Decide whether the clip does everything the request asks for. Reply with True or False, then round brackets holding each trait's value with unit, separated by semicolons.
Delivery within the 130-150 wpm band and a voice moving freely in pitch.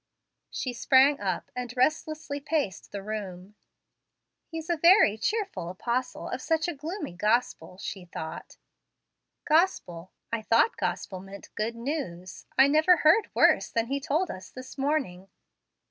True (140 wpm; 8.0 semitones)